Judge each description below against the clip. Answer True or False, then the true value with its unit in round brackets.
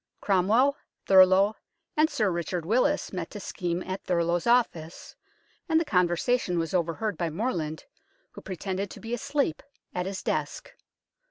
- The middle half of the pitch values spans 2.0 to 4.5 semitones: False (4.9 semitones)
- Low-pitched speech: False (190 Hz)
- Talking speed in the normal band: True (150 wpm)